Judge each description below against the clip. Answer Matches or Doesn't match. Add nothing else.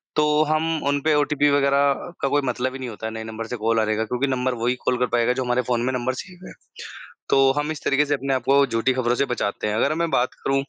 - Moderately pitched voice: Doesn't match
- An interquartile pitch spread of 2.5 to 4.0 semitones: Matches